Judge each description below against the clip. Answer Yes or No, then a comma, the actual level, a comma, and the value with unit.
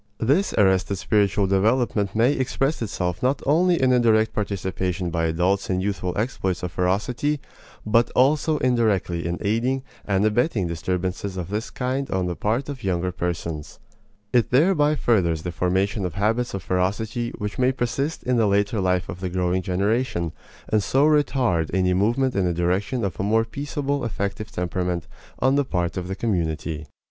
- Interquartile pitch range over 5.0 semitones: Yes, wide, 5.4 semitones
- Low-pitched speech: Yes, low, 100 Hz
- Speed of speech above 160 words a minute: Yes, average, 170 wpm